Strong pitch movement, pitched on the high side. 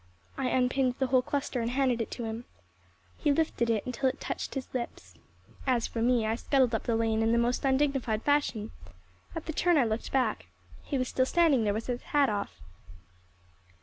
No: average, 2.9 semitones; very high, 250 Hz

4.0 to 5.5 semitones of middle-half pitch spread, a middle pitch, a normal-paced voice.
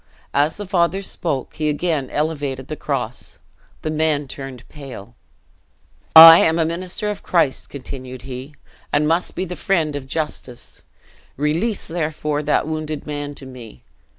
No: average, 3.3 semitones; medium, 150 Hz; average, 150 wpm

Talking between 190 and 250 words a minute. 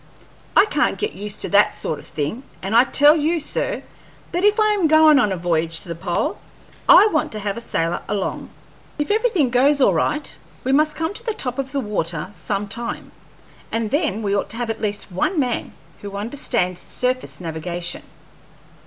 Yes: average, 195 wpm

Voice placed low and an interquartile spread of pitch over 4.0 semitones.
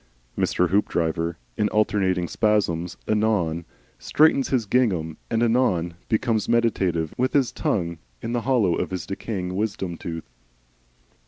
Yes: low, 100 Hz; average, 5.0 semitones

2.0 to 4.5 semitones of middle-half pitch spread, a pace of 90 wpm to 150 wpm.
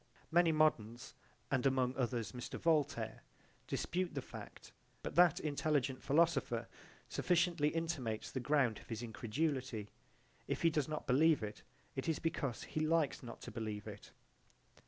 No: average, 5.1 semitones; average, 145 wpm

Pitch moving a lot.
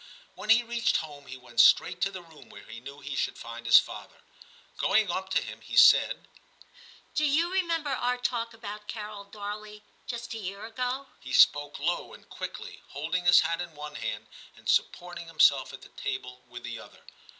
Yes: wide, 8.0 semitones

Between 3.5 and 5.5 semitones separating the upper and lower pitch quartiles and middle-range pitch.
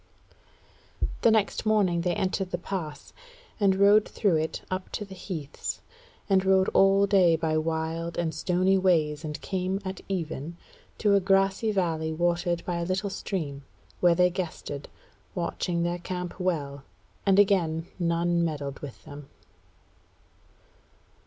No: average, 3.0 semitones; medium, 175 Hz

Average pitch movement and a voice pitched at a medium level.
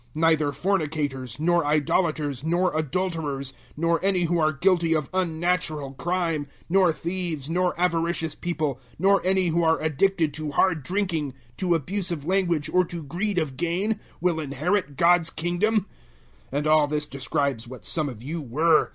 Yes: average, 3.2 semitones; medium, 165 Hz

